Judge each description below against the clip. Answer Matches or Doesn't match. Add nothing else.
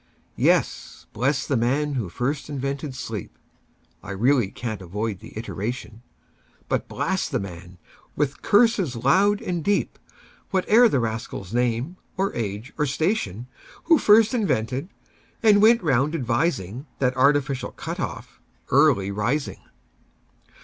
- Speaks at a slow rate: Matches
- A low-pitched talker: Matches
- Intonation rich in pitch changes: Matches